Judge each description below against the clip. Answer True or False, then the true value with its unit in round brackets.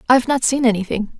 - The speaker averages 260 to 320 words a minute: False (200 wpm)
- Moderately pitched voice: False (240 Hz)